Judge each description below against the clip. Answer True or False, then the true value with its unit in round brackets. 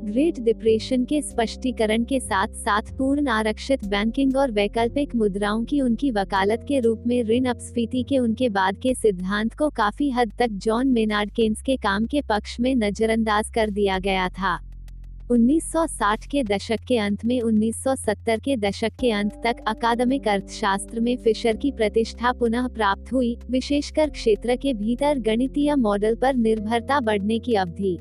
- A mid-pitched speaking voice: False (230 Hz)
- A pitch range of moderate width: True (3.2 semitones)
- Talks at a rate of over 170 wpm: False (160 wpm)